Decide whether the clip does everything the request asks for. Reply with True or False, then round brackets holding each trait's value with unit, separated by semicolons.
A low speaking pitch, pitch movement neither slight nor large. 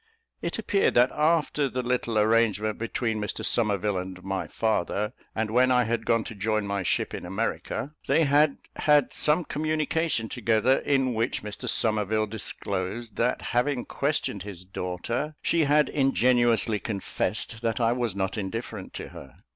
True (115 Hz; 3.9 semitones)